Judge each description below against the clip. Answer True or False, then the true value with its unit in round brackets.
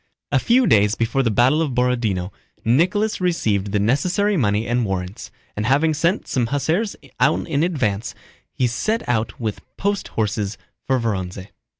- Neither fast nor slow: True (160 wpm)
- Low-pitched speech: True (120 Hz)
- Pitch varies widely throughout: True (7.4 semitones)